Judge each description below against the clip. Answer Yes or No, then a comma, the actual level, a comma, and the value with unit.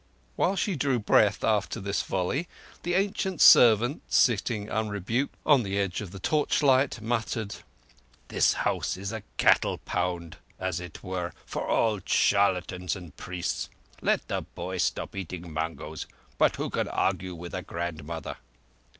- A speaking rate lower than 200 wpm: Yes, average, 140 wpm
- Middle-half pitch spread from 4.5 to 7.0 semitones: Yes, average, 4.8 semitones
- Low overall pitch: Yes, low, 100 Hz